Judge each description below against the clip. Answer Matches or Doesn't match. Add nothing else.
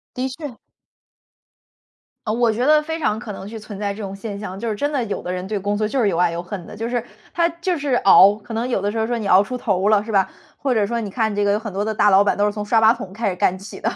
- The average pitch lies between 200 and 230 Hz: Matches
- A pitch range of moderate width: Matches